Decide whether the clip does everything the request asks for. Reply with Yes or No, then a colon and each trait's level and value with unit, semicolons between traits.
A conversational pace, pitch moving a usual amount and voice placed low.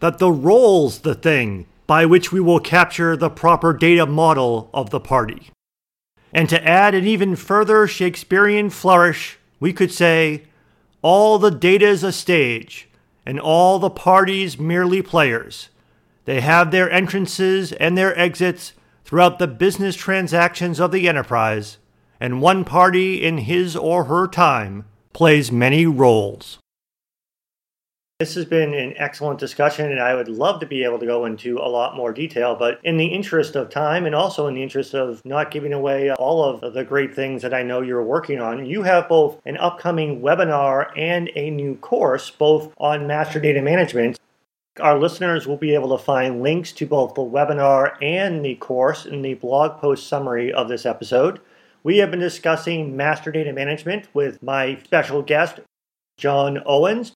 No: average, 170 wpm; average, 4.5 semitones; medium, 155 Hz